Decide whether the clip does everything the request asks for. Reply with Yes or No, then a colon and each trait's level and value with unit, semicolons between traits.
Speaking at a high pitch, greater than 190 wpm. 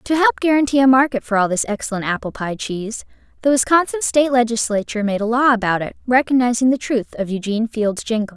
Yes: high, 240 Hz; average, 200 wpm